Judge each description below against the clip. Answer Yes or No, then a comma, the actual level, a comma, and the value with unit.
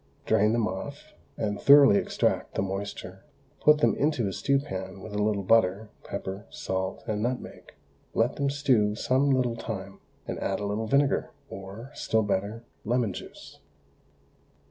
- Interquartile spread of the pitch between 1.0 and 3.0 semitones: No, average, 4.7 semitones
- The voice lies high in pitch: No, low, 110 Hz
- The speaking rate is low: No, average, 155 wpm